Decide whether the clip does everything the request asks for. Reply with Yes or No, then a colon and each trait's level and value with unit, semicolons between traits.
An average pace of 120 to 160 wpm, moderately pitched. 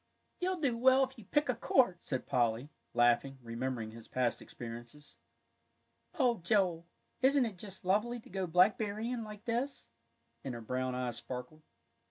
Yes: average, 155 wpm; medium, 180 Hz